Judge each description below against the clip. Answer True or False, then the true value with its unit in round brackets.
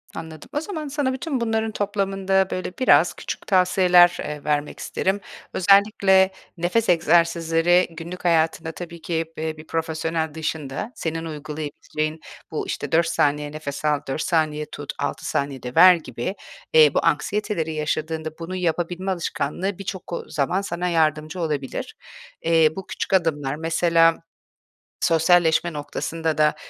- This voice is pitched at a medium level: True (165 Hz)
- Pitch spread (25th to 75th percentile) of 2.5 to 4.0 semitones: True (3.1 semitones)